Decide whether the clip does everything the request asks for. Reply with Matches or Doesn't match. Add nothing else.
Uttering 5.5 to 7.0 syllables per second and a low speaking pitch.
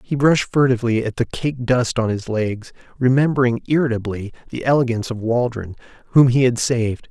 Matches